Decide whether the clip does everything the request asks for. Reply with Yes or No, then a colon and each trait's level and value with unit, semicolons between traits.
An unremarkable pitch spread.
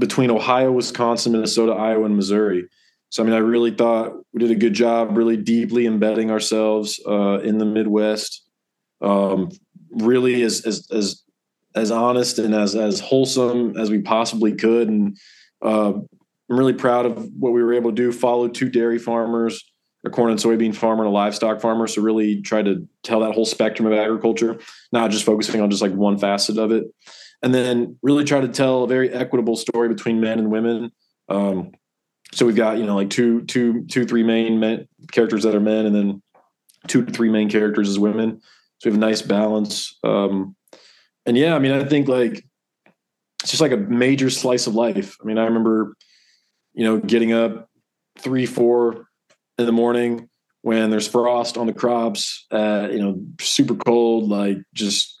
No: narrow, 1.8 semitones